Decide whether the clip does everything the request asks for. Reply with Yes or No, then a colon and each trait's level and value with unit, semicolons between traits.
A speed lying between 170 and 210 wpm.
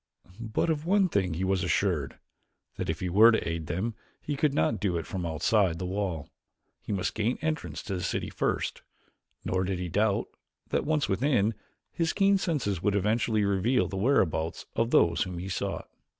Yes: average, 190 wpm